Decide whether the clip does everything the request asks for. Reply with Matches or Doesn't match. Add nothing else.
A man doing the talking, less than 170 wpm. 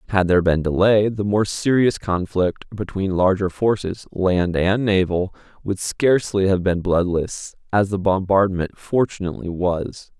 Matches